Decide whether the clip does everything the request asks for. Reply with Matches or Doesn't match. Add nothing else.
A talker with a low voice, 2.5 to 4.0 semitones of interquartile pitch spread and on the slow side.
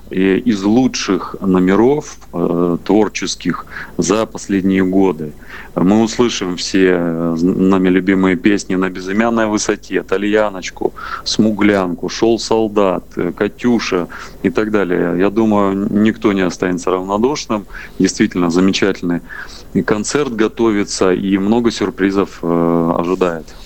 Matches